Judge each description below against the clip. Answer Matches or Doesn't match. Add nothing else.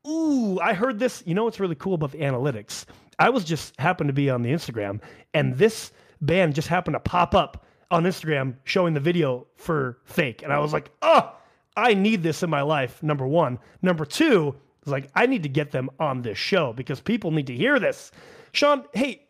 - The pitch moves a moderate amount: Doesn't match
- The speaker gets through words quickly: Matches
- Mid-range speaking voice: Matches